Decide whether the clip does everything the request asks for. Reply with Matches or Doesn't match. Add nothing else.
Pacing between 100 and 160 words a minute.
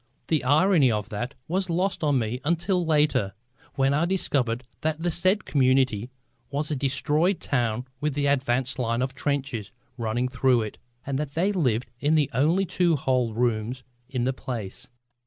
Doesn't match